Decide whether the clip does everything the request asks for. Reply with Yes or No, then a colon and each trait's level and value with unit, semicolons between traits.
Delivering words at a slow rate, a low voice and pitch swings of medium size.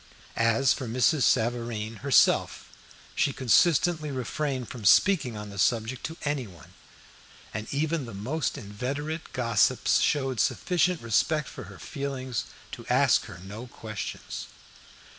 Yes: slow, 125 wpm; low, 125 Hz; average, 4.9 semitones